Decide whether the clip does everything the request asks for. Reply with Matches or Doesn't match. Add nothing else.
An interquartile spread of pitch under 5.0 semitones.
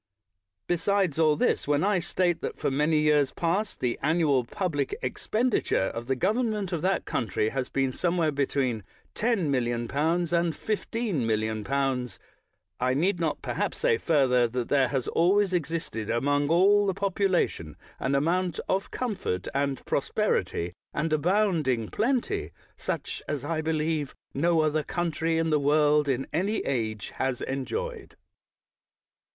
Doesn't match